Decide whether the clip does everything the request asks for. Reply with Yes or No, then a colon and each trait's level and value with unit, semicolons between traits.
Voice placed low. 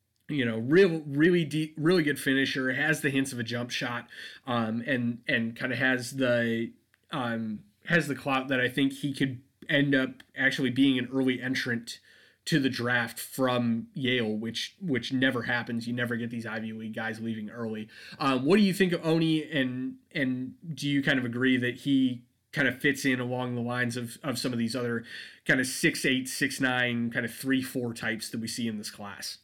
Yes: low, 130 Hz